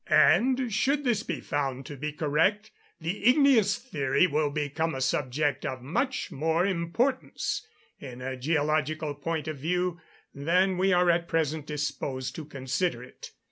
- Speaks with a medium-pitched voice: Yes, medium, 160 Hz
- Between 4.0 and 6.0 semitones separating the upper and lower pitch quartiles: Yes, average, 4.9 semitones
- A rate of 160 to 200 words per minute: No, average, 150 wpm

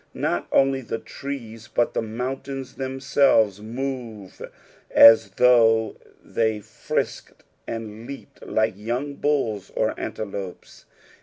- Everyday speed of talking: No, slow, 105 wpm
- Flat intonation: No, average, 3.4 semitones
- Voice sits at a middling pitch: No, low, 115 Hz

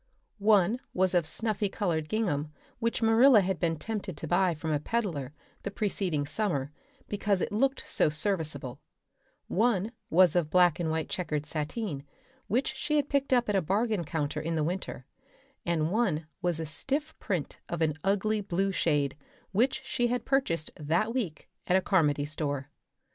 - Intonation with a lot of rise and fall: Yes, wide, 5.7 semitones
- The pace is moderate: Yes, average, 170 wpm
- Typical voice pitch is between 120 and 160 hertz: No, medium, 180 Hz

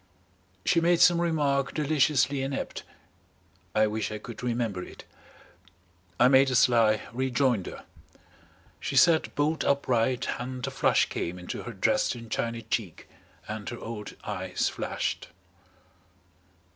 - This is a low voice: Yes, low, 125 Hz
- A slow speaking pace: Yes, slow, 125 wpm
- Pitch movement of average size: Yes, average, 4.1 semitones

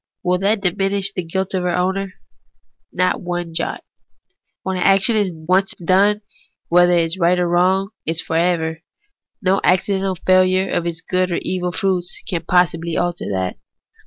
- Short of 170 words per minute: Yes, average, 160 wpm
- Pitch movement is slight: Yes, narrow, 1.6 semitones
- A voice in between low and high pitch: Yes, medium, 180 Hz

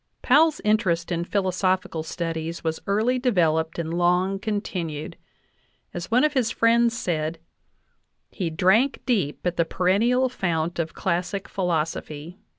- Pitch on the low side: No, medium, 180 Hz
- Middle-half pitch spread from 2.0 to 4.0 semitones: No, average, 4.8 semitones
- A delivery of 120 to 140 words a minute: Yes, slow, 135 wpm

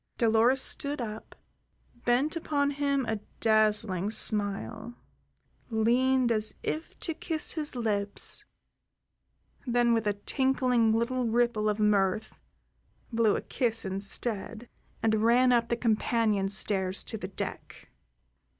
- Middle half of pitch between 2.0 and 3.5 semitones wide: Yes, average, 2.9 semitones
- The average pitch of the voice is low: No, high, 230 Hz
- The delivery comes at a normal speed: No, slow, 120 wpm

